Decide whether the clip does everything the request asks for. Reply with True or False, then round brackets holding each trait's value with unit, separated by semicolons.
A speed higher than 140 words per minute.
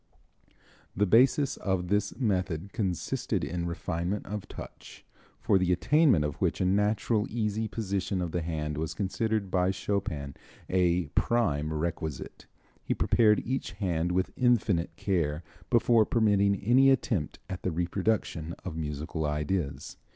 False (135 wpm)